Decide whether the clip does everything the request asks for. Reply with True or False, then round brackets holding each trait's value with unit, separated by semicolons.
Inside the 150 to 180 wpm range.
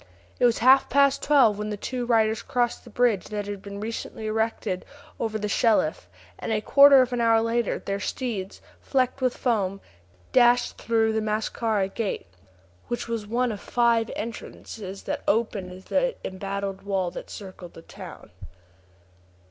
True (160 wpm)